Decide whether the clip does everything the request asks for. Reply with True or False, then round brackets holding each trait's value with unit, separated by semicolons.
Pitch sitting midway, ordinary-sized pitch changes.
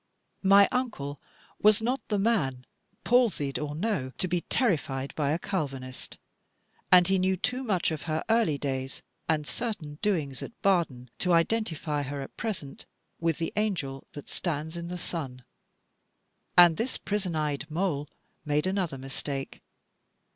False (165 Hz; 5.7 semitones)